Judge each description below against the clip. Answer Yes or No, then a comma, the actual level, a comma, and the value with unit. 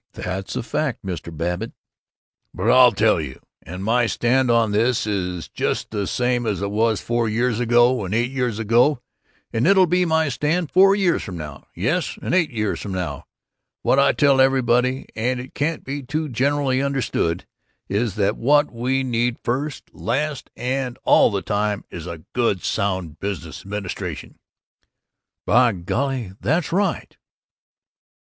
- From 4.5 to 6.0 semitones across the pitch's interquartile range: Yes, average, 4.8 semitones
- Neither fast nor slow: Yes, average, 160 wpm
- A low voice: Yes, low, 120 Hz